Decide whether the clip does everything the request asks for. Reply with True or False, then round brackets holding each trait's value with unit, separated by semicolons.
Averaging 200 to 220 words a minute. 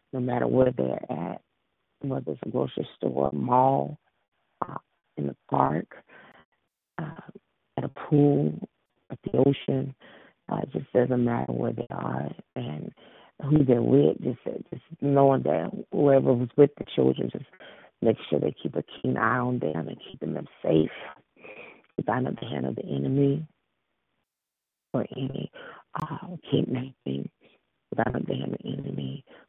False (155 wpm)